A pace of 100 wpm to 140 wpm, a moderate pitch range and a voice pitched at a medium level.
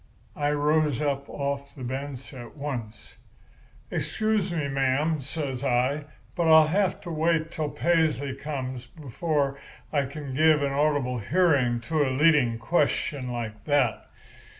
Yes: slow, 135 wpm; average, 3.1 semitones; medium, 145 Hz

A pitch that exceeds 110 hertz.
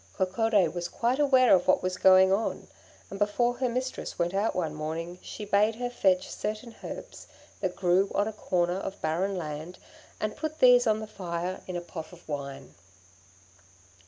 Yes: high, 190 Hz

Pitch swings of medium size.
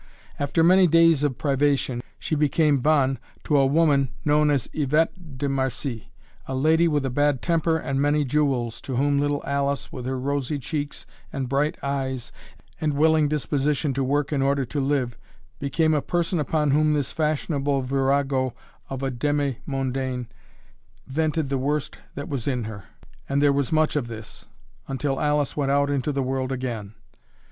No: narrow, 2.0 semitones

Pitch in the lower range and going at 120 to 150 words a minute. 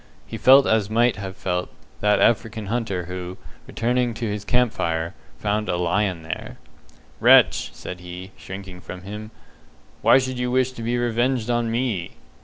No: low, 105 Hz; average, 165 wpm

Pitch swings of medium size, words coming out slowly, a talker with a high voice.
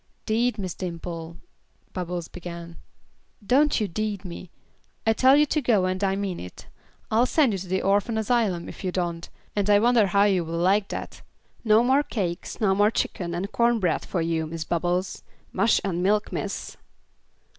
No: average, 4.0 semitones; average, 180 wpm; high, 195 Hz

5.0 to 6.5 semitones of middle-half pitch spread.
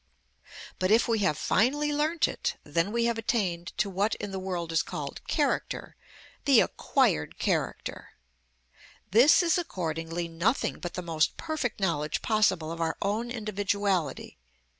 Yes: wide, 5.5 semitones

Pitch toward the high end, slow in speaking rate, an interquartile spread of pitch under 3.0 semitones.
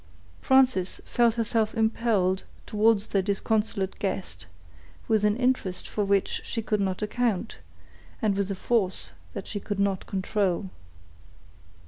Yes: high, 210 Hz; slow, 130 wpm; narrow, 2.6 semitones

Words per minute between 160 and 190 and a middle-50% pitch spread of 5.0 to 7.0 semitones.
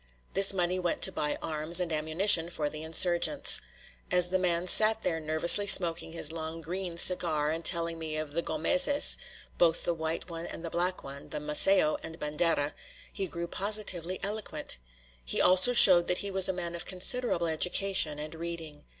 No: average, 180 wpm; average, 2.7 semitones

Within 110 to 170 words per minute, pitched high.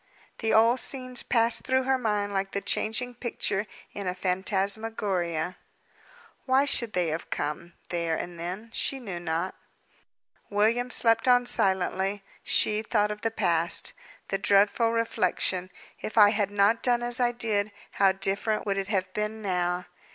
Yes: average, 155 wpm; high, 205 Hz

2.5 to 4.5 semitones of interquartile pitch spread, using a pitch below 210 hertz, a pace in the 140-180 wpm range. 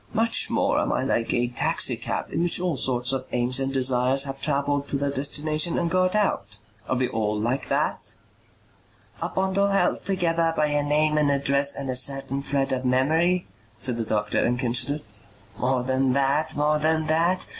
No: average, 3.6 semitones; medium, 140 Hz; average, 190 wpm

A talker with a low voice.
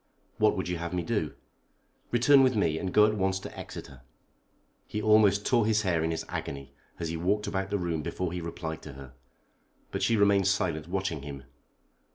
Yes: very low, 90 Hz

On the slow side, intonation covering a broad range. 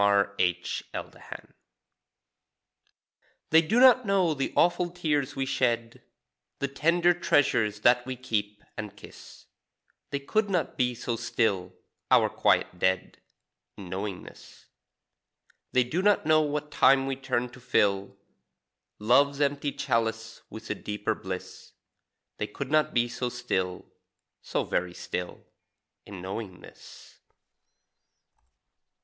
Yes: slow, 125 wpm; wide, 6.1 semitones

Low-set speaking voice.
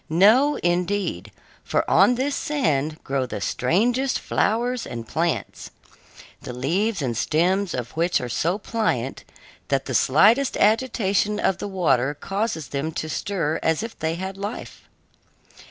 No: medium, 185 Hz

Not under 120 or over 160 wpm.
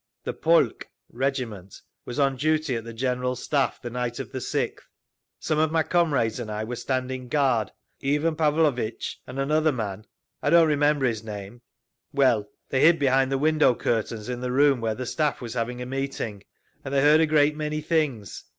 No: average, 180 wpm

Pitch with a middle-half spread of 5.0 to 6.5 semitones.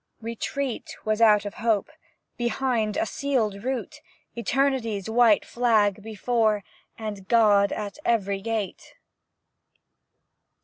No: narrow, 2.6 semitones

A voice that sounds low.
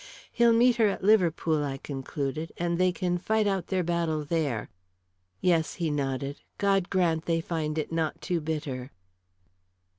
No: medium, 165 Hz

